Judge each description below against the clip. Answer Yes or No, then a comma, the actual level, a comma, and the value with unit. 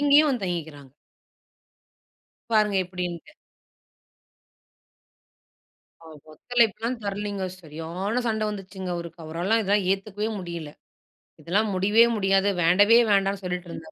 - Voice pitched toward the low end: No, high, 195 Hz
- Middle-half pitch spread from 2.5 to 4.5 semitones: Yes, average, 3.6 semitones